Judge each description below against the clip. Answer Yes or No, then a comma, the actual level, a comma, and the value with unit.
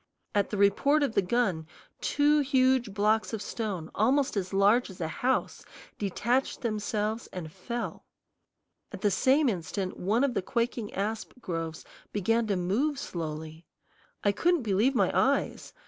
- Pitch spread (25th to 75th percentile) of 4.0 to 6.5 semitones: Yes, average, 4.7 semitones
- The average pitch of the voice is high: Yes, high, 215 Hz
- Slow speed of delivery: No, average, 150 wpm